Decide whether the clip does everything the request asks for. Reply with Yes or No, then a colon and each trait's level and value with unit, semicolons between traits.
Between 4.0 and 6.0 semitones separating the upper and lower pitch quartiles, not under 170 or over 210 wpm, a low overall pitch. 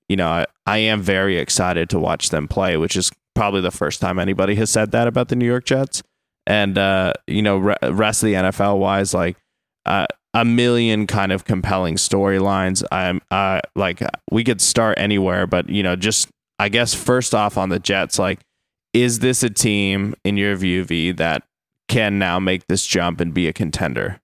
No: average, 2.8 semitones; average, 200 wpm; low, 100 Hz